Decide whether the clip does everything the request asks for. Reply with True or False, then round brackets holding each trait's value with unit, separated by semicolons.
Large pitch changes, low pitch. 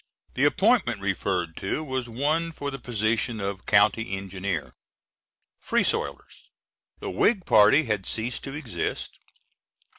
True (5.9 semitones; 115 Hz)